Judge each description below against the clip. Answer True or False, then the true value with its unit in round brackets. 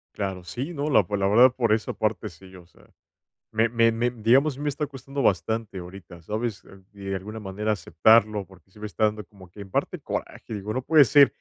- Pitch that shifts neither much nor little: True (3.8 semitones)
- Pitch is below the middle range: True (105 Hz)